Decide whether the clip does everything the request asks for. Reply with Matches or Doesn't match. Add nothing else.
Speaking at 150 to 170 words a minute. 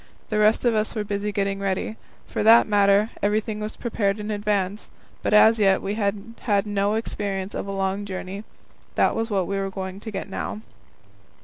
Doesn't match